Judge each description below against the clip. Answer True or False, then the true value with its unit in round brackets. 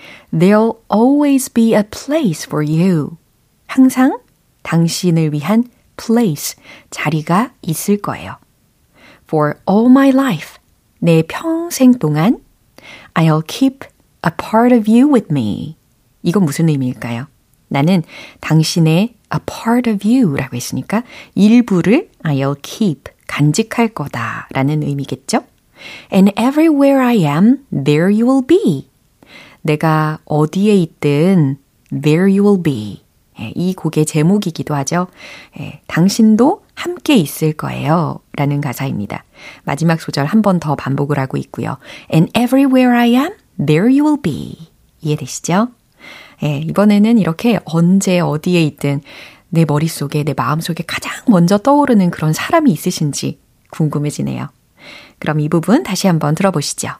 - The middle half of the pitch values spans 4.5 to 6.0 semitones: False (7.6 semitones)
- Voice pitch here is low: False (175 Hz)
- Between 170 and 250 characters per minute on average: False (345 characters per minute)